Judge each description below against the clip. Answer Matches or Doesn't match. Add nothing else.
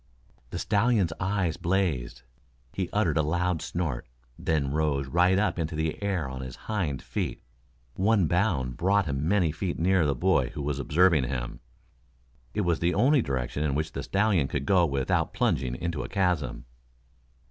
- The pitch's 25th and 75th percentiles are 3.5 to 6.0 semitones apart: Matches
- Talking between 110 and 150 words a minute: Doesn't match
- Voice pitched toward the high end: Doesn't match